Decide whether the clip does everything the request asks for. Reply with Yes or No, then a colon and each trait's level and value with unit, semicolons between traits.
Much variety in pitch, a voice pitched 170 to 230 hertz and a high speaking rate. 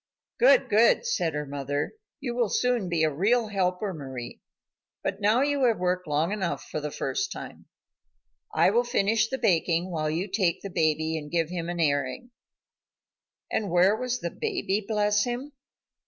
No: wide, 6.6 semitones; high, 190 Hz; average, 170 wpm